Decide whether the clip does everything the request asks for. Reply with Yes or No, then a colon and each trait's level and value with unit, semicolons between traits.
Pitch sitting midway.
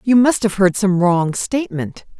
No: high, 200 Hz